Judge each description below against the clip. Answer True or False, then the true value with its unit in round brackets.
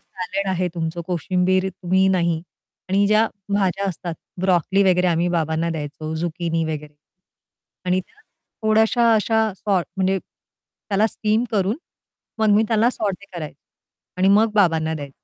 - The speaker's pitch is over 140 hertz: True (185 Hz)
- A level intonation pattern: False (3.6 semitones)